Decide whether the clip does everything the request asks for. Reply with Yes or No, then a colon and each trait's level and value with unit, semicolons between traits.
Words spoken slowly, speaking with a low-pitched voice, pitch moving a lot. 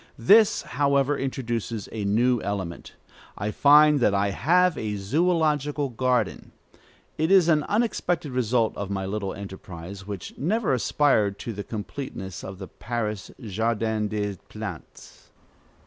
Yes: slow, 130 wpm; low, 115 Hz; wide, 6.4 semitones